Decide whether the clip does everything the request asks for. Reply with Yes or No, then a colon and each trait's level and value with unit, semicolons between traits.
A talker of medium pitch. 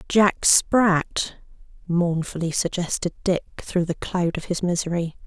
Yes: medium, 175 Hz